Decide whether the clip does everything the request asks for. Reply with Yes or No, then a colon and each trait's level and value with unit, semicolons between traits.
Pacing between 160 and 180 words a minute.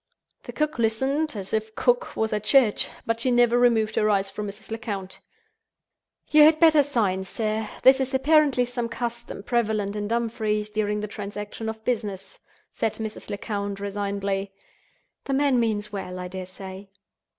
Yes: average, 165 wpm